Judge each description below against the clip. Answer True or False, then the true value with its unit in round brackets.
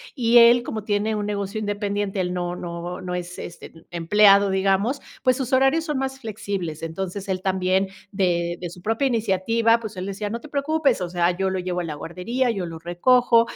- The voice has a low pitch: False (200 Hz)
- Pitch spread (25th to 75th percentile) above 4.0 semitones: True (4.5 semitones)